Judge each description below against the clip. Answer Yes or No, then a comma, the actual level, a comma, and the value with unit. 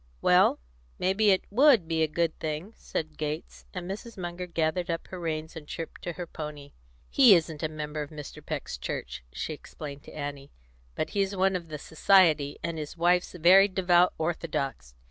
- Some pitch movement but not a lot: Yes, average, 3.2 semitones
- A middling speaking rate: Yes, average, 185 wpm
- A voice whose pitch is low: No, medium, 165 Hz